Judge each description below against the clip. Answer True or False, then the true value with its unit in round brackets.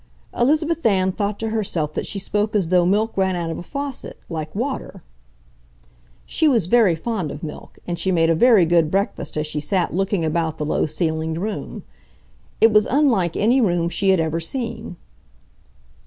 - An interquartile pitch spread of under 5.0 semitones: False (5.3 semitones)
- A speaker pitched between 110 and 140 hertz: False (190 Hz)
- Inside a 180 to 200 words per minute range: True (185 wpm)